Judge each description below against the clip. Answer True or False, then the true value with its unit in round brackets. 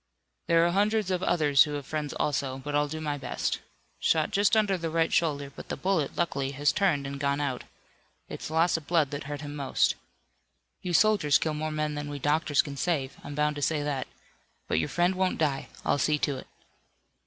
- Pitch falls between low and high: True (150 Hz)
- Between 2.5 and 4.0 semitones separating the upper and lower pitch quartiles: True (2.8 semitones)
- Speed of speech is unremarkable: False (210 wpm)